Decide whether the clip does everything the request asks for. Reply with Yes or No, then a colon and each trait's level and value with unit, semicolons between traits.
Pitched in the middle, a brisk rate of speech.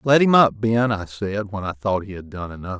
No: low, 105 Hz; fast, 280 wpm